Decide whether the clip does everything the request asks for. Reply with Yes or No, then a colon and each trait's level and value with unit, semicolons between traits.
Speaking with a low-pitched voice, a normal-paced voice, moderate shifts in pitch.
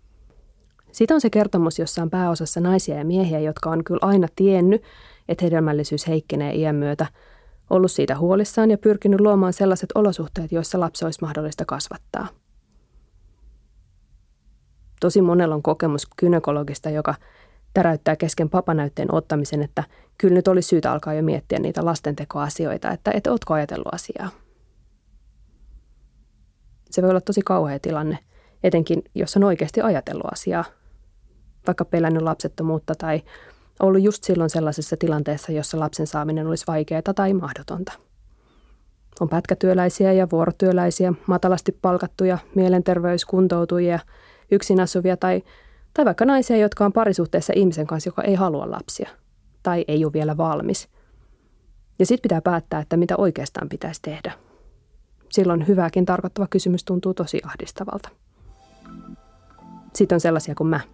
No: medium, 175 Hz; average, 130 wpm; average, 3.1 semitones